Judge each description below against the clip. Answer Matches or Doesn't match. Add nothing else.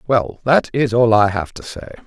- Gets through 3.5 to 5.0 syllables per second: Matches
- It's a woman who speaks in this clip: Doesn't match